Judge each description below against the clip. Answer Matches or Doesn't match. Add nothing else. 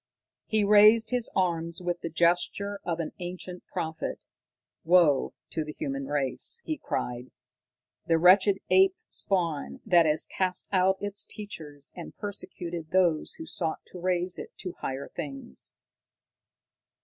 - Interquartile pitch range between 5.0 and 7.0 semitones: Doesn't match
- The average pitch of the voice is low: Doesn't match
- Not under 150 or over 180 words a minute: Doesn't match